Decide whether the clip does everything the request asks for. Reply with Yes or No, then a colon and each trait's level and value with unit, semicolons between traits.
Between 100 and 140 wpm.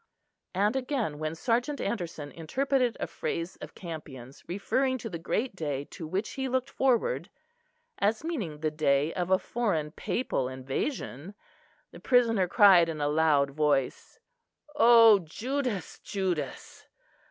Yes: slow, 135 wpm